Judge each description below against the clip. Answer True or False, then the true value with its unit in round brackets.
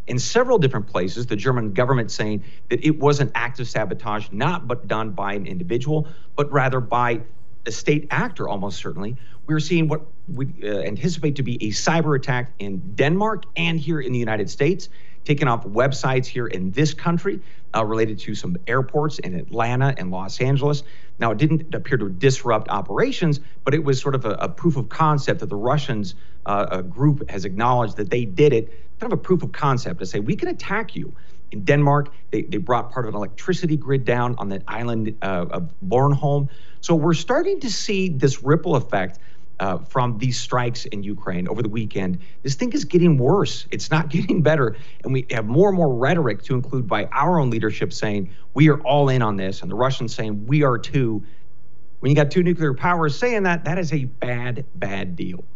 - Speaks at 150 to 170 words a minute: False (205 wpm)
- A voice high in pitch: False (135 Hz)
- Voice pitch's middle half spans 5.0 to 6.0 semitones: True (5.3 semitones)